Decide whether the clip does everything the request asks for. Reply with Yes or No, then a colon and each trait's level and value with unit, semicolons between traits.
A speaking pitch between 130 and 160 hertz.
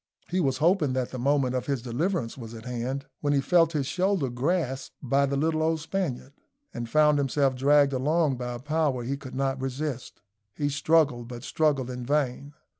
Yes: medium, 140 Hz